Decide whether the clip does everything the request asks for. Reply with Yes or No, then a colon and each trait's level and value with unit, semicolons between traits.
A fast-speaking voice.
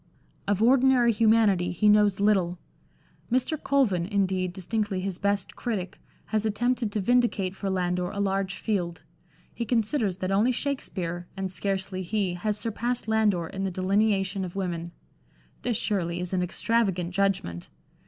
No: average, 145 wpm